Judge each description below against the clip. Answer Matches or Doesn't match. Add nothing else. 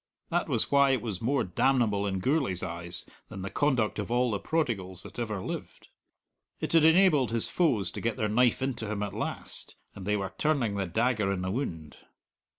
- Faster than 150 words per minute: Matches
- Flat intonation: Doesn't match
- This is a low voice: Matches